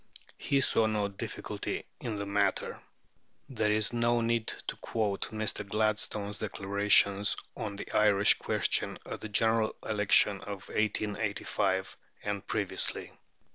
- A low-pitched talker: Yes, low, 105 Hz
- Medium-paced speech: No, slow, 125 wpm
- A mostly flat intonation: Yes, narrow, 1.4 semitones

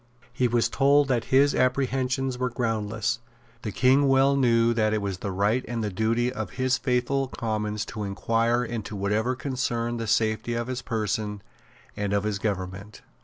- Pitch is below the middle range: Yes, low, 115 Hz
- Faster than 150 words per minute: Yes, average, 170 wpm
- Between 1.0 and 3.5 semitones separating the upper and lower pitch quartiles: Yes, average, 3.1 semitones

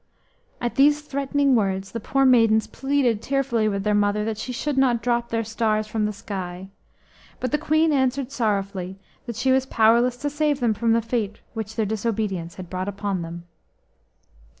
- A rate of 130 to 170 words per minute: No, average, 185 wpm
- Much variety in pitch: No, average, 4.3 semitones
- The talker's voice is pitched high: Yes, high, 225 Hz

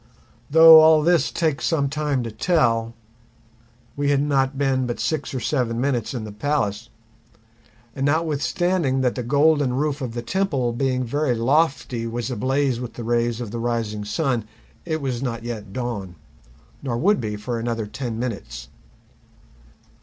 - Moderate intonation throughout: Yes, average, 3.8 semitones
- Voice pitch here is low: Yes, low, 125 Hz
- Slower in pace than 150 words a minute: No, average, 160 wpm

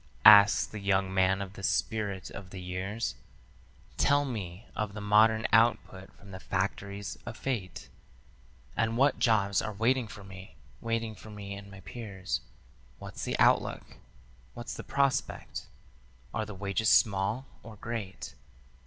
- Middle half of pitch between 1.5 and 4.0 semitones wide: Yes, average, 2.7 semitones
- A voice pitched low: Yes, low, 100 Hz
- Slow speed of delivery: No, average, 145 wpm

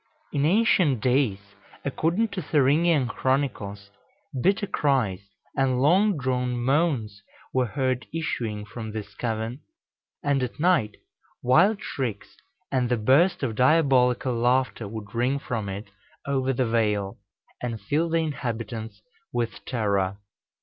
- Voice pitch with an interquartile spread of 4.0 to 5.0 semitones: Yes, average, 4.5 semitones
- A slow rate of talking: Yes, slow, 130 wpm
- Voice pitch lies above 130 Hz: No, low, 125 Hz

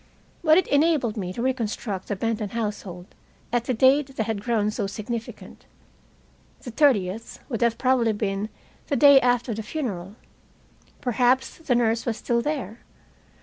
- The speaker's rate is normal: Yes, average, 150 wpm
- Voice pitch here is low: No, high, 235 Hz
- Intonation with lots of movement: No, average, 3.6 semitones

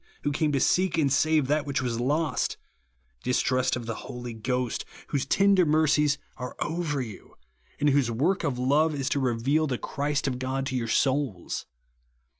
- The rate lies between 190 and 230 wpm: Yes, average, 195 wpm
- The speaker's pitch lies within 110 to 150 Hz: Yes, medium, 140 Hz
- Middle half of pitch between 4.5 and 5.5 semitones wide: No, average, 3.1 semitones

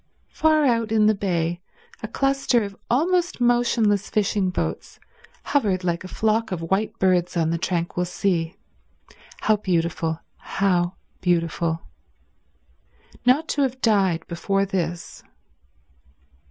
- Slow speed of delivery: Yes, slow, 120 wpm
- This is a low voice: No, high, 195 Hz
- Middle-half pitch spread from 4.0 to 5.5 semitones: Yes, average, 4.8 semitones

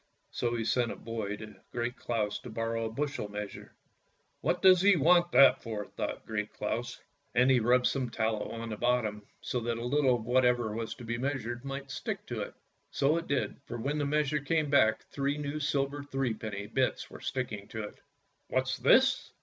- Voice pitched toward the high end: No, low, 125 Hz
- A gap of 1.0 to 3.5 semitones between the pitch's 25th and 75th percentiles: No, average, 3.9 semitones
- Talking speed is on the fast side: Yes, fast, 210 wpm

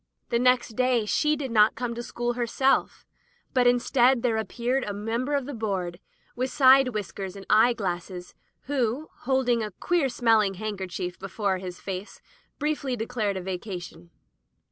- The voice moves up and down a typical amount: Yes, average, 4.3 semitones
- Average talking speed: Yes, average, 155 wpm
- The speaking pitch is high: Yes, high, 230 Hz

